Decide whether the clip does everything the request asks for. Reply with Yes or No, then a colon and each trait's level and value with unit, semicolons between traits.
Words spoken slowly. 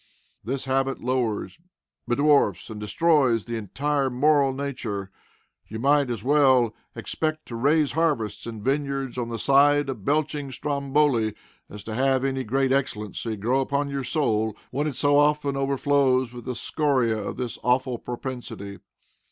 No: average, 150 wpm